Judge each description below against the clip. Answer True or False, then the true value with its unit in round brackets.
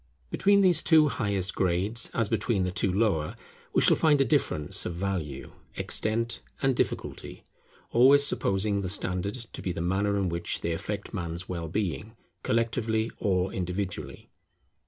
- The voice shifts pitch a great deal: False (4.2 semitones)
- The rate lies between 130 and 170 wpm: True (155 wpm)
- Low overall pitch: True (100 Hz)